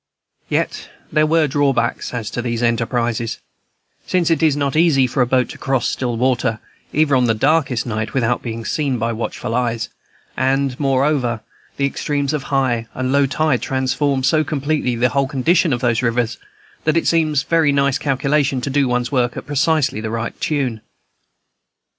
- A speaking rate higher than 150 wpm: Yes, average, 175 wpm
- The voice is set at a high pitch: No, low, 130 Hz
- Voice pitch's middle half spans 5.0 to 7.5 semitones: No, average, 3.2 semitones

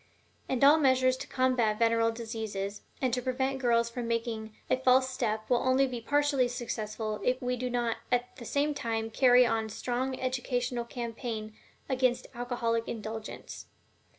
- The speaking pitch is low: No, high, 245 Hz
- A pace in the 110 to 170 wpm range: Yes, average, 160 wpm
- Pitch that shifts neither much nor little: No, narrow, 2.2 semitones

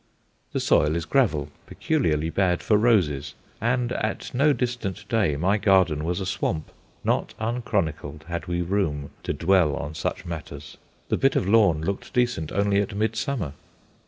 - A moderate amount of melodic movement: No, wide, 6.1 semitones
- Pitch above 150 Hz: No, very low, 95 Hz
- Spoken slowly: No, average, 160 wpm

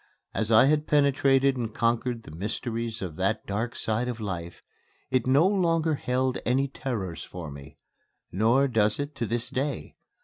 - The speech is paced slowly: No, average, 165 wpm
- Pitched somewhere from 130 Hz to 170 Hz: No, low, 120 Hz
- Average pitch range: Yes, average, 4.2 semitones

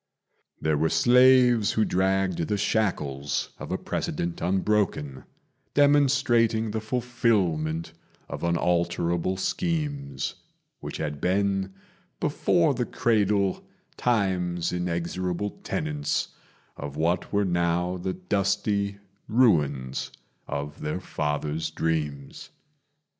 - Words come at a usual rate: No, slow, 95 wpm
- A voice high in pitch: No, very low, 95 Hz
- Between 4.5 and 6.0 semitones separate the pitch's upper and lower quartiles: Yes, average, 4.8 semitones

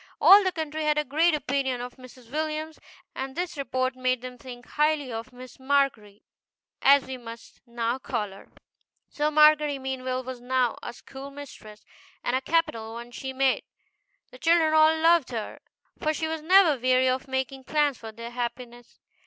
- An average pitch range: Yes, average, 3.7 semitones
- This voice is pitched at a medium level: No, very high, 265 Hz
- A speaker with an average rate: Yes, average, 170 wpm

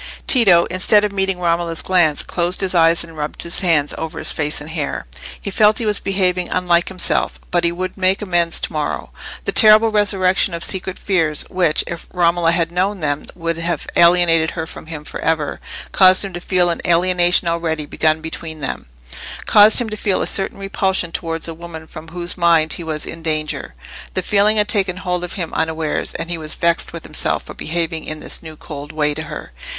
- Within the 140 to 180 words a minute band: No, fast, 205 wpm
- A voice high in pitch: No, medium, 170 Hz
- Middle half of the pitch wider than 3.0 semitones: No, narrow, 2.6 semitones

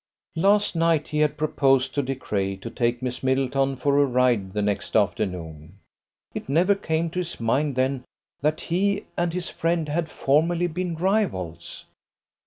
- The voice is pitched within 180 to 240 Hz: No, medium, 140 Hz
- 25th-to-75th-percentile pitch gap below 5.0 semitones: No, average, 5.3 semitones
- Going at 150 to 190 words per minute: Yes, average, 165 wpm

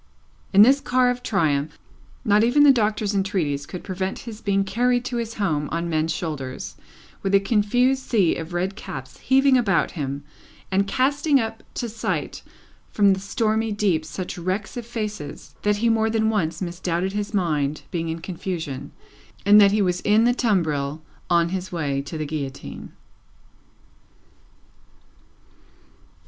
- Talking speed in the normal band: Yes, average, 155 wpm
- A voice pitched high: Yes, high, 195 Hz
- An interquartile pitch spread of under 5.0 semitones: No, average, 5.3 semitones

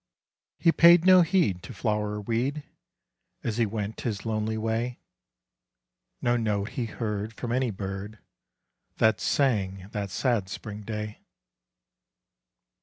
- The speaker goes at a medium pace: No, slow, 125 wpm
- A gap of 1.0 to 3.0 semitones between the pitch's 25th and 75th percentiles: Yes, average, 2.7 semitones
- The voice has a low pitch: Yes, low, 110 Hz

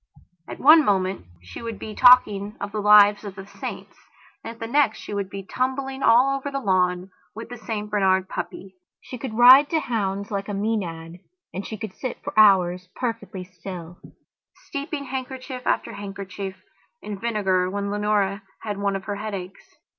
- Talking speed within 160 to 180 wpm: Yes, average, 175 wpm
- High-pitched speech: Yes, high, 205 Hz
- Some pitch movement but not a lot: Yes, average, 3.5 semitones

